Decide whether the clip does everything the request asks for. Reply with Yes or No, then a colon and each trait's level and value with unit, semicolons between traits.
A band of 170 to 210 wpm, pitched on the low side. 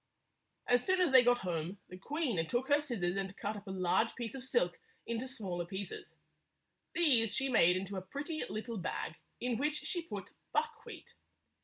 No: average, 180 wpm; high, 230 Hz